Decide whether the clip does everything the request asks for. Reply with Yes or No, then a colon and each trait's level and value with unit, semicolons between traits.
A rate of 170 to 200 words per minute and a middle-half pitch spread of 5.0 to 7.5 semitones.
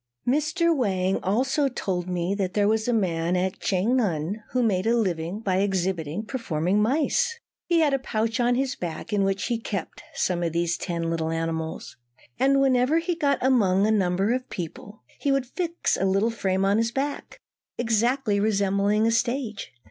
Yes: average, 180 wpm; wide, 5.5 semitones